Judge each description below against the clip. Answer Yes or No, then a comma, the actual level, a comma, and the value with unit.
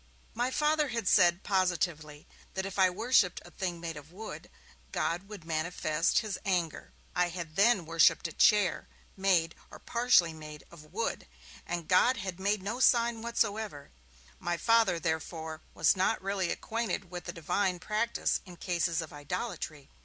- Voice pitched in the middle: Yes, medium, 180 Hz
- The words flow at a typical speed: Yes, average, 160 wpm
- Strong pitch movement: No, average, 4.2 semitones